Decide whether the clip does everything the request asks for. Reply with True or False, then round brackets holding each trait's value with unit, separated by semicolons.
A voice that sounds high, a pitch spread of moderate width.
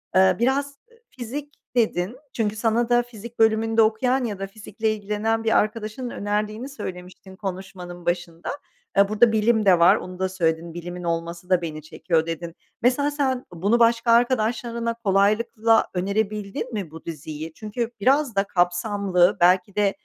True (210 Hz; 4.4 semitones)